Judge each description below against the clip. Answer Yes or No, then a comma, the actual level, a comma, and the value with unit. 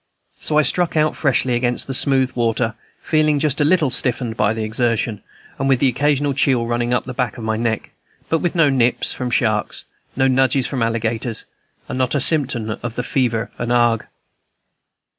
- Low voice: Yes, low, 125 Hz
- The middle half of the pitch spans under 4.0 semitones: Yes, average, 3.1 semitones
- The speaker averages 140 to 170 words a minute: No, average, 185 wpm